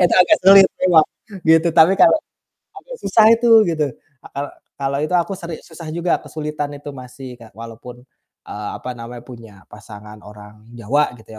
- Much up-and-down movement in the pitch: Yes, wide, 6.6 semitones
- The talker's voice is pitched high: No, medium, 145 Hz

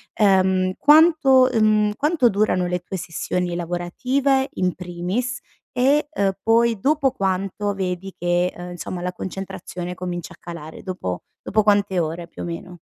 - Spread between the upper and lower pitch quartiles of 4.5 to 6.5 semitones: Yes, average, 4.9 semitones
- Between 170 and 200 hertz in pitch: Yes, high, 190 Hz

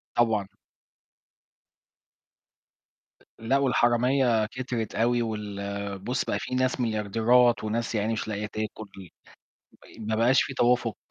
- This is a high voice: No, low, 115 Hz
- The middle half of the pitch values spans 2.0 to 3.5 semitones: Yes, narrow, 2.4 semitones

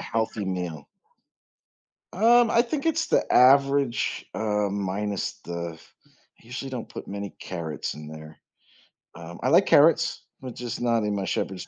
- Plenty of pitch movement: Yes, wide, 6.5 semitones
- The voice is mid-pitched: No, low, 105 Hz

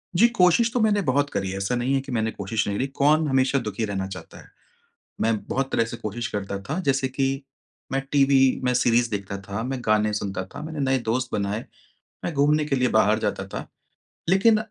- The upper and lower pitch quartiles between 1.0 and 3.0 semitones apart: No, average, 4.9 semitones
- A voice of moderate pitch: No, low, 130 Hz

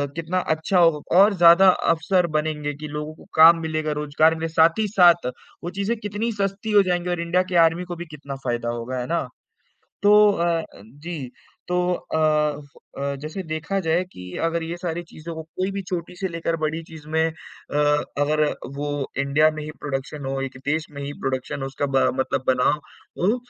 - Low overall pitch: No, medium, 160 Hz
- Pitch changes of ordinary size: Yes, average, 3.1 semitones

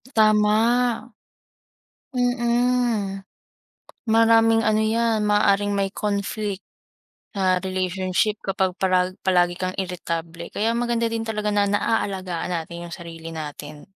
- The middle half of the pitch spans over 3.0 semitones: Yes, average, 3.4 semitones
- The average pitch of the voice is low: No, high, 200 Hz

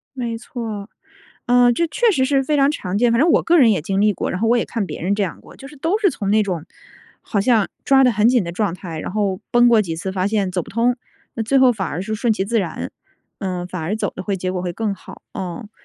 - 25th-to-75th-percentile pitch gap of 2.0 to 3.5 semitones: No, average, 4.5 semitones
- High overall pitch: Yes, high, 215 Hz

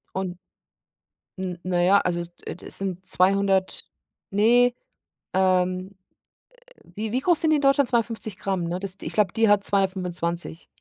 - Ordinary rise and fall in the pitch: Yes, average, 3.0 semitones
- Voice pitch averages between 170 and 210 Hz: Yes, high, 190 Hz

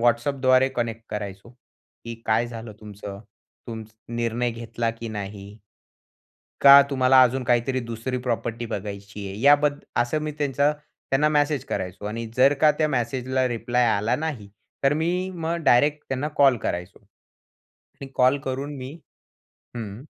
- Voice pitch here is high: No, low, 120 Hz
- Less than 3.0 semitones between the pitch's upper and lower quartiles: No, average, 3.7 semitones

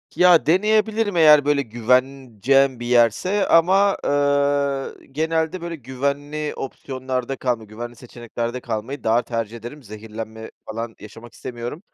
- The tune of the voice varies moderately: Yes, average, 4.5 semitones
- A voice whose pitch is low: Yes, low, 130 Hz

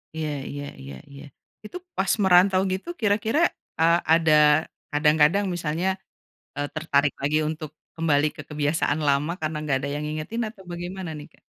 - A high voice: No, medium, 155 Hz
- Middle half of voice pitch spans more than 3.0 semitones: Yes, average, 3.5 semitones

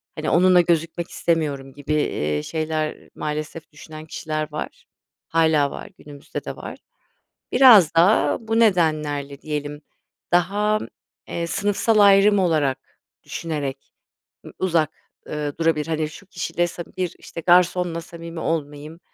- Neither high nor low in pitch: Yes, medium, 160 Hz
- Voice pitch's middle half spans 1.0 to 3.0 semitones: Yes, average, 2.7 semitones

